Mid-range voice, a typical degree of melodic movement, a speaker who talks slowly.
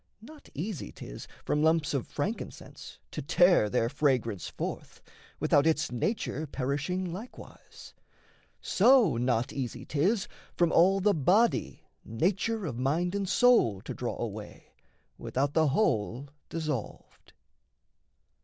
No: medium, 155 Hz; wide, 6.6 semitones; slow, 120 wpm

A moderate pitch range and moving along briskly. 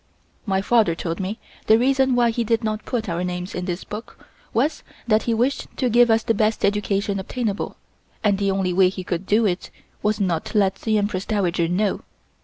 Yes: average, 3.2 semitones; fast, 210 wpm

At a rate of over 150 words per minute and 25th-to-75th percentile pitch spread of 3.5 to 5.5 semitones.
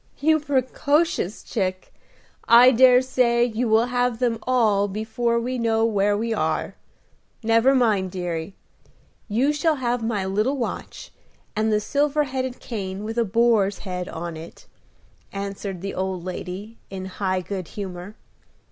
No: average, 145 wpm; average, 4.2 semitones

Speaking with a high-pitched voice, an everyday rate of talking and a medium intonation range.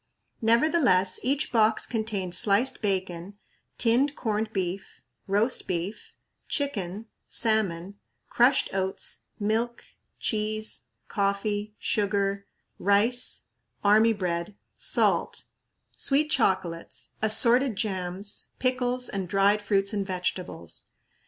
No: high, 205 Hz; slow, 95 wpm; average, 3.2 semitones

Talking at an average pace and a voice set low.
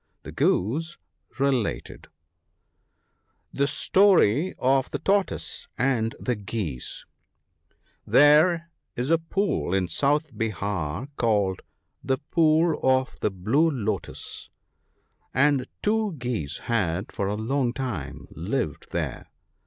No: slow, 115 wpm; low, 130 Hz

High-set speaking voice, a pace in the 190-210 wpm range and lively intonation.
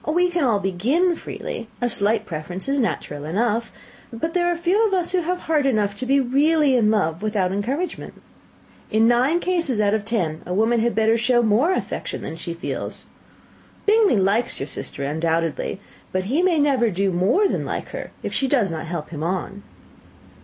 Yes: high, 230 Hz; average, 195 wpm; wide, 7.7 semitones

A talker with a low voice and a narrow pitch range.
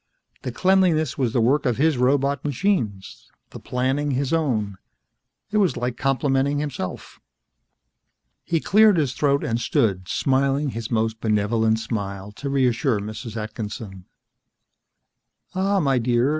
No: low, 130 Hz; average, 4.5 semitones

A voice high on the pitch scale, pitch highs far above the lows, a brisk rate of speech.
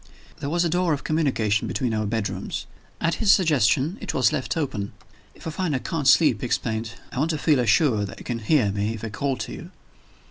No: low, 135 Hz; wide, 6.2 semitones; fast, 225 wpm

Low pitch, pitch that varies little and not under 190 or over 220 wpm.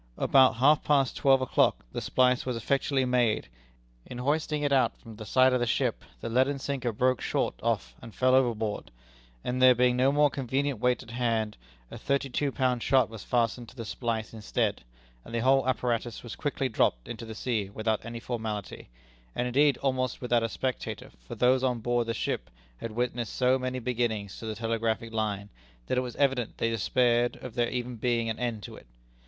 Yes: low, 125 Hz; narrow, 2.2 semitones; average, 200 wpm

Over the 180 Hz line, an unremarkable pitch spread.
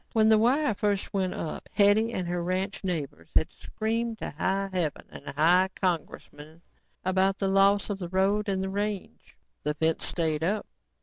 Yes: high, 190 Hz; average, 3.2 semitones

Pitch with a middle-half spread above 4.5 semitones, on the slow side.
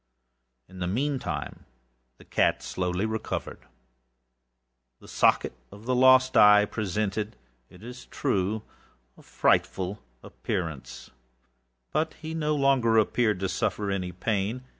Yes: average, 4.9 semitones; slow, 120 wpm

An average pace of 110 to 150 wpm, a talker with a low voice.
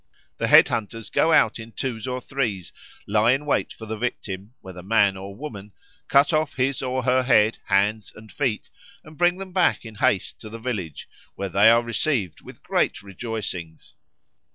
No: average, 180 wpm; low, 115 Hz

